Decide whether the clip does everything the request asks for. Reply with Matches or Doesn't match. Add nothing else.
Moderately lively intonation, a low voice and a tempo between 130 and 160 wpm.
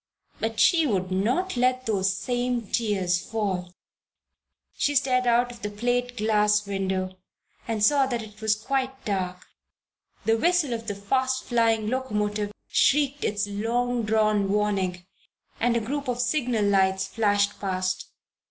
Doesn't match